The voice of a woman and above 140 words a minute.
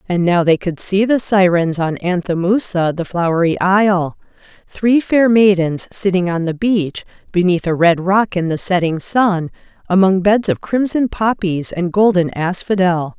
Yes: female; average, 160 wpm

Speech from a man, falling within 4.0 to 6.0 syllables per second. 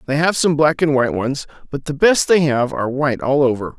Yes: male; 5.9 syllables/s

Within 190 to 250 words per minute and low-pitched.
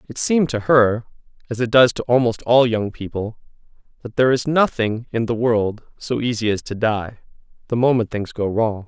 Yes: average, 195 wpm; low, 115 Hz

